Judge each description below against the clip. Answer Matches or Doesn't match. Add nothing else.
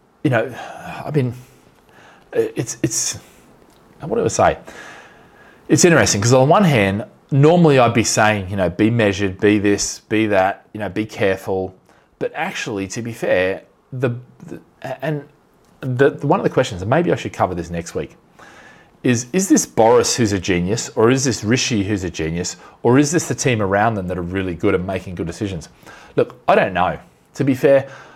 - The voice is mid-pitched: Doesn't match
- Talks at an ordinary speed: Matches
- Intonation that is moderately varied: Doesn't match